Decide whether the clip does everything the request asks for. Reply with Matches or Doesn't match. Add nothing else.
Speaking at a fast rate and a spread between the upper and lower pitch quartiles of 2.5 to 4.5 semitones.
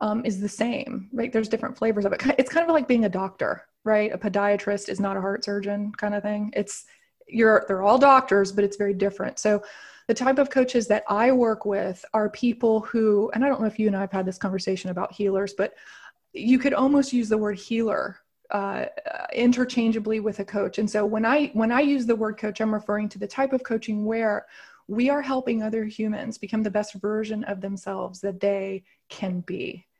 Matches